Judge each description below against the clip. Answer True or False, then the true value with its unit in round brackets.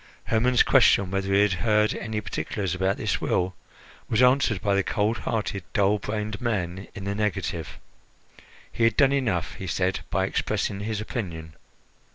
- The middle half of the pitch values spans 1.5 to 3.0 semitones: True (2.4 semitones)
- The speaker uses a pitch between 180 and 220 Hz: False (105 Hz)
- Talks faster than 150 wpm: True (165 wpm)